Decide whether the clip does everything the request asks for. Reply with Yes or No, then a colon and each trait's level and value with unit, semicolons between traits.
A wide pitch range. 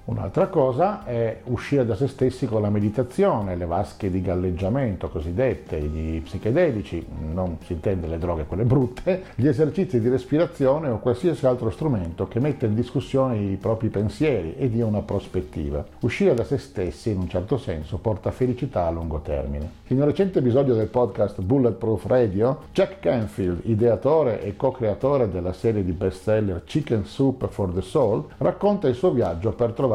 Yes: wide, 5.8 semitones